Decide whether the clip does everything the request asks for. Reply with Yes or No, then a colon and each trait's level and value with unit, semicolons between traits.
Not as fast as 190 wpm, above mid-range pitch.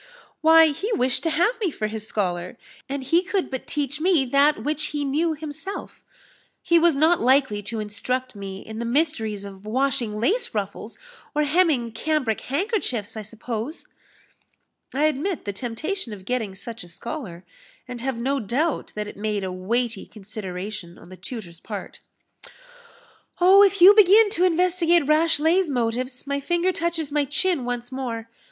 Yes: average, 165 wpm; very high, 265 Hz